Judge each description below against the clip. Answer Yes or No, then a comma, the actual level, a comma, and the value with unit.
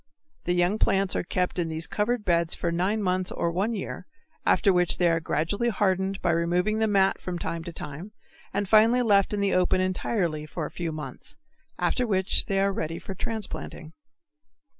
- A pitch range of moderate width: Yes, average, 3.2 semitones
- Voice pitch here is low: No, medium, 185 Hz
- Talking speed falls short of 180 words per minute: No, average, 190 wpm